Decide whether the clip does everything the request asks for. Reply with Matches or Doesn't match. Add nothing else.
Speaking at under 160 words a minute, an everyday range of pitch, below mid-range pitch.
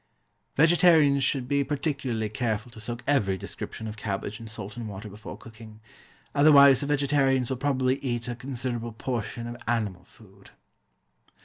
Matches